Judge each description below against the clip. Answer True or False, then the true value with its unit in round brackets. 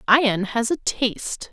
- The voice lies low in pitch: False (240 Hz)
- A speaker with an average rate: True (160 wpm)